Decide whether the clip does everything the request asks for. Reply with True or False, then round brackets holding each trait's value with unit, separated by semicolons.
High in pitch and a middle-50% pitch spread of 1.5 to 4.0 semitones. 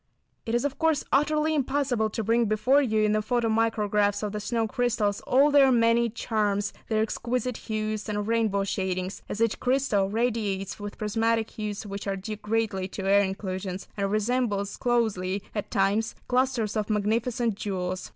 True (215 Hz; 2.7 semitones)